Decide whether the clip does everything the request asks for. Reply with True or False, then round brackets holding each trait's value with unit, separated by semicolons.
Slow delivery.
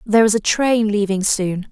False (210 wpm)